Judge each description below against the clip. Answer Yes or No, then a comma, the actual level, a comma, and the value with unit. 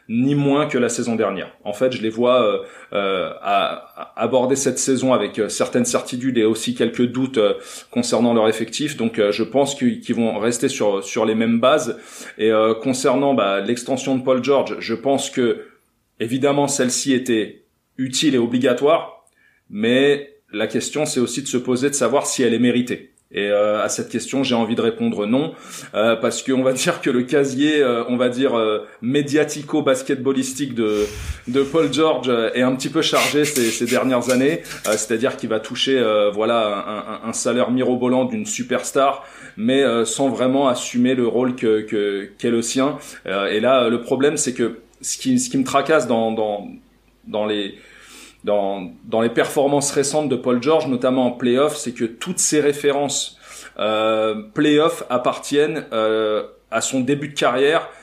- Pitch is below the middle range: Yes, low, 125 Hz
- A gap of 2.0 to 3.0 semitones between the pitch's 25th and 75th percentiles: No, average, 3.8 semitones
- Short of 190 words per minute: Yes, average, 180 wpm